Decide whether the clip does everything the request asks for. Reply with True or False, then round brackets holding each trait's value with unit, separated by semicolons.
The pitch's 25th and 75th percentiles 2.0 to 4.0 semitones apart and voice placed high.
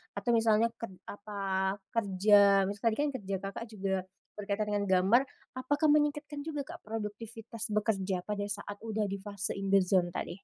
True (2.7 semitones; 205 Hz)